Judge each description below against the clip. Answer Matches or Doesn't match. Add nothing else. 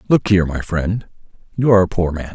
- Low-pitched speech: Matches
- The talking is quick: Matches